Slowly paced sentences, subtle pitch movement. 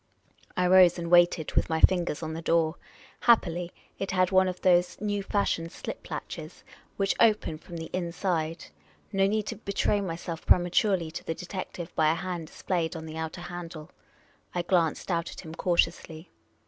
No: average, 175 wpm; narrow, 2.3 semitones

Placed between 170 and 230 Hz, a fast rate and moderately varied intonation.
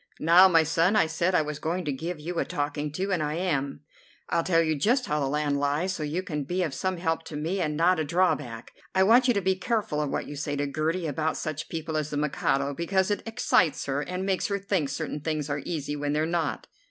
No: medium, 160 Hz; fast, 250 wpm; average, 3.7 semitones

